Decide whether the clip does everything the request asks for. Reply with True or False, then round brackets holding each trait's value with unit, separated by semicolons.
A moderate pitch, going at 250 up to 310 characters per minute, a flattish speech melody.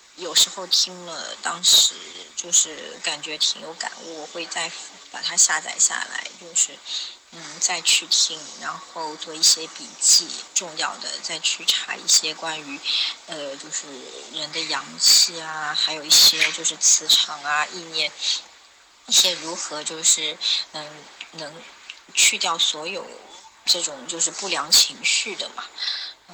False (160 Hz; 205 characters per minute; 1.9 semitones)